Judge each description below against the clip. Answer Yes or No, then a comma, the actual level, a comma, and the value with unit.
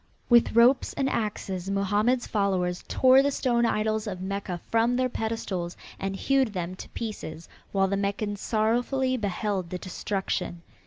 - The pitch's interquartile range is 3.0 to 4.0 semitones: Yes, average, 3.7 semitones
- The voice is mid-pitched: No, high, 210 Hz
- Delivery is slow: No, average, 150 wpm